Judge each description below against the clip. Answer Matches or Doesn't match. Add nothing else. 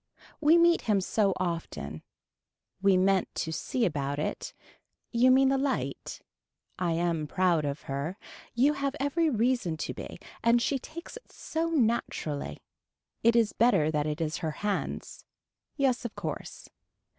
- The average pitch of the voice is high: Matches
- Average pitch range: Doesn't match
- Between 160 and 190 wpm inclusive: Doesn't match